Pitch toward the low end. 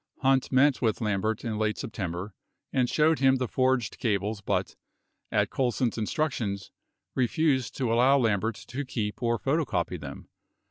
Yes: low, 120 Hz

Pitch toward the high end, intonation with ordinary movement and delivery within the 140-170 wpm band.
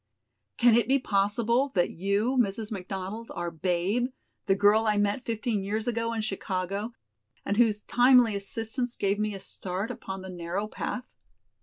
Yes: high, 210 Hz; average, 3.1 semitones; average, 160 wpm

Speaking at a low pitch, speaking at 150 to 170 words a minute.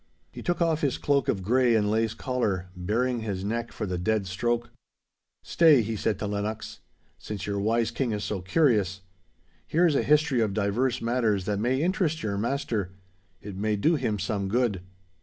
No: low, 110 Hz; average, 185 wpm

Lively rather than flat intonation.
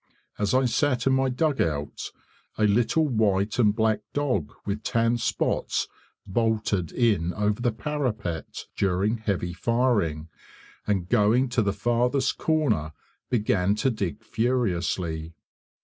No: average, 4.4 semitones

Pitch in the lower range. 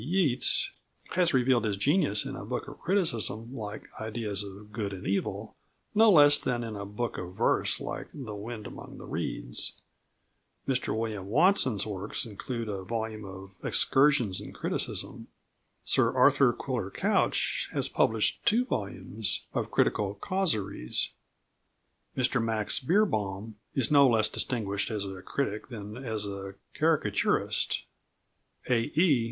Yes: low, 110 Hz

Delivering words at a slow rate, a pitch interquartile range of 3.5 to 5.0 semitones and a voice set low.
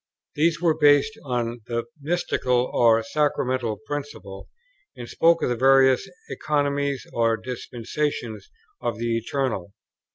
Yes: slow, 120 wpm; average, 3.8 semitones; low, 130 Hz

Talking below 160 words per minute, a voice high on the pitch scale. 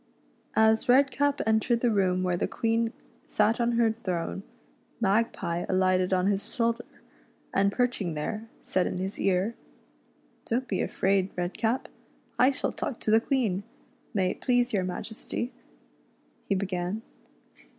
Yes: average, 140 wpm; high, 215 Hz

